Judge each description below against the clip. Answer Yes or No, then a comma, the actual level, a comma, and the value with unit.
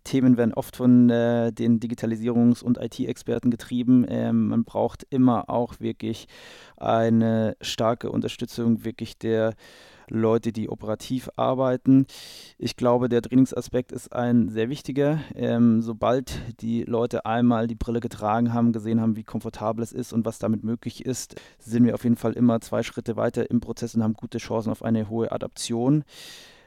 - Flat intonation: Yes, narrow, 1.2 semitones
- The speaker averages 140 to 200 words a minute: Yes, average, 160 wpm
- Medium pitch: No, low, 115 Hz